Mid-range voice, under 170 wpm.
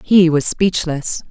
Yes: medium, 170 Hz; average, 140 wpm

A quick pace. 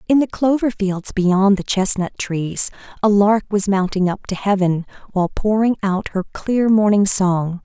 No: average, 175 wpm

